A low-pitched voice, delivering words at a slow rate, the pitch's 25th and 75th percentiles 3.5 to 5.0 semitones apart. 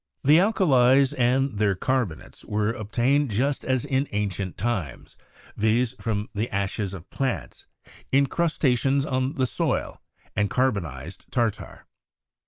Yes: low, 120 Hz; slow, 125 wpm; average, 4.7 semitones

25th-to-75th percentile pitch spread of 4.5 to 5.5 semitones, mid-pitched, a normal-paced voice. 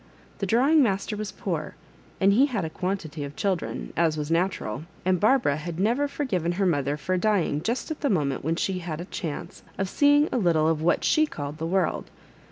No: average, 5.1 semitones; medium, 180 Hz; fast, 210 wpm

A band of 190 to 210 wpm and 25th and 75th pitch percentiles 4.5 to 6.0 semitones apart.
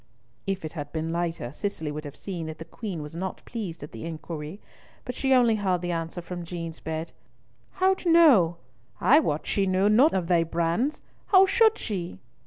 Yes: average, 195 wpm; average, 5.2 semitones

